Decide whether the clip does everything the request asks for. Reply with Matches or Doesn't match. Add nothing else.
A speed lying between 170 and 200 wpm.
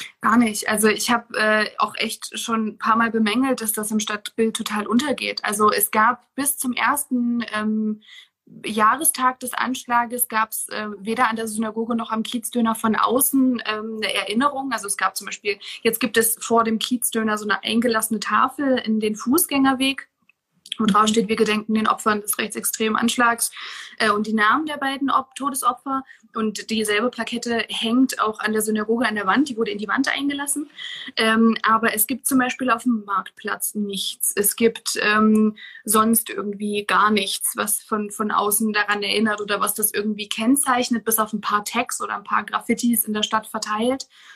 Matches